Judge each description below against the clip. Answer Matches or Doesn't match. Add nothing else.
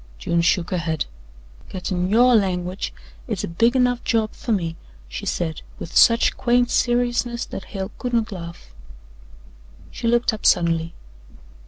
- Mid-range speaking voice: Doesn't match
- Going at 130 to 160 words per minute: Matches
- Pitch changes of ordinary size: Doesn't match